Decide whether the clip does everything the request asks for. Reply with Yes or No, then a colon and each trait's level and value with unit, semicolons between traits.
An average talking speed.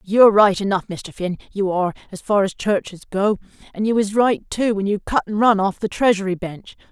No: fast, 225 wpm